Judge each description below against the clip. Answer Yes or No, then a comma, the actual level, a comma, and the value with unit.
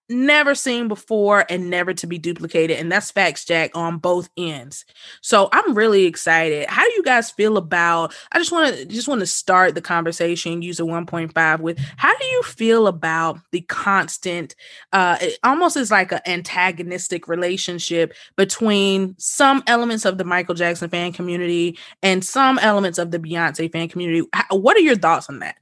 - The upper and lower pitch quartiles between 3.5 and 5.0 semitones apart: Yes, average, 4.1 semitones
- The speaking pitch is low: No, medium, 180 Hz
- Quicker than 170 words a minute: Yes, average, 180 wpm